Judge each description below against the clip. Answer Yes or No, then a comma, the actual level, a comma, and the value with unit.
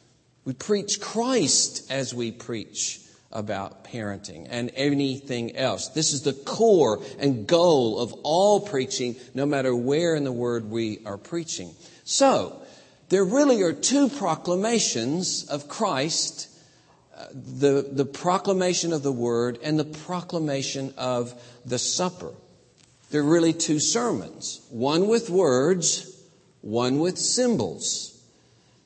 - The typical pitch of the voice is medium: Yes, medium, 145 Hz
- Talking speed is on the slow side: Yes, slow, 125 wpm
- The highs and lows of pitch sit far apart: Yes, wide, 6.4 semitones